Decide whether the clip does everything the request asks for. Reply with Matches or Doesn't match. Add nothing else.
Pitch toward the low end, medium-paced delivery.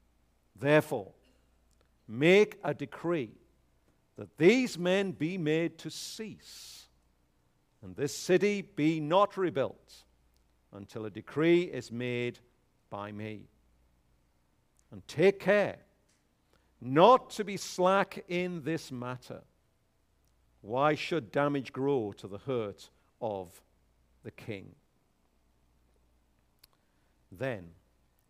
Doesn't match